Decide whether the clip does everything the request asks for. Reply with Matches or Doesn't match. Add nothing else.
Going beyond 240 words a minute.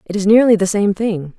Matches